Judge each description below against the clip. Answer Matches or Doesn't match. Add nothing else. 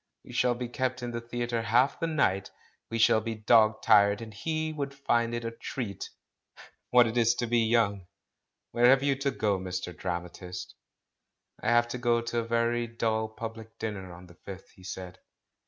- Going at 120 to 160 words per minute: Doesn't match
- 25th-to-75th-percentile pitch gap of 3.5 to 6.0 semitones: Doesn't match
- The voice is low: Matches